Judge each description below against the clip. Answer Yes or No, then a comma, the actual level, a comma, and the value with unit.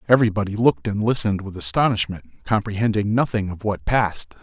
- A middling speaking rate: Yes, average, 150 wpm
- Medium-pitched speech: No, low, 105 Hz